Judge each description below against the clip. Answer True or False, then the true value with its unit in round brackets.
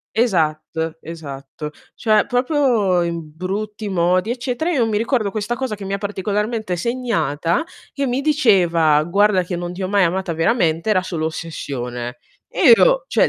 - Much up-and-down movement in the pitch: True (5.7 semitones)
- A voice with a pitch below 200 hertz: True (190 Hz)